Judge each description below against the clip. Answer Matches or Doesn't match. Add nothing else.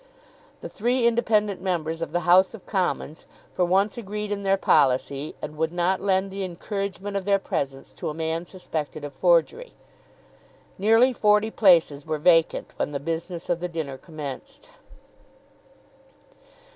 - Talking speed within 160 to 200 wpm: Doesn't match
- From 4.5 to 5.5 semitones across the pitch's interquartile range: Doesn't match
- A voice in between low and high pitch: Matches